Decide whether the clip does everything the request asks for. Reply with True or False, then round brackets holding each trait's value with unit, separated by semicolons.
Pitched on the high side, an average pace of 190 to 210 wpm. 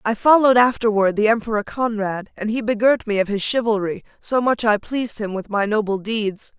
True (220 Hz; 200 wpm)